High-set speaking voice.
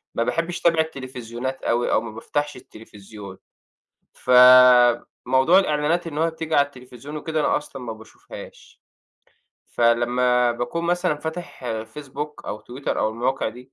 No: low, 130 Hz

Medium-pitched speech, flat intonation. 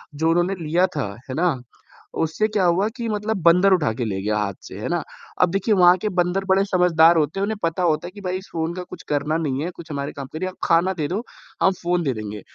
No: medium, 175 Hz; average, 3.7 semitones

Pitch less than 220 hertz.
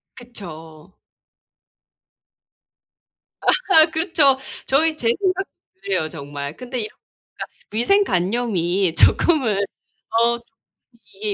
No: high, 235 Hz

